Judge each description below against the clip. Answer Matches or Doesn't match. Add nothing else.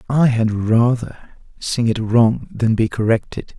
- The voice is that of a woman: Doesn't match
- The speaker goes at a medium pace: Matches